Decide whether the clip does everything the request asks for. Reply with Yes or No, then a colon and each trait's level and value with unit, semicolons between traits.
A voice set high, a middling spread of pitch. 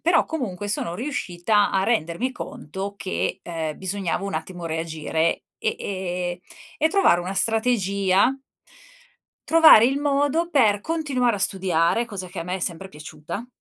No: high, 195 Hz; wide, 5.9 semitones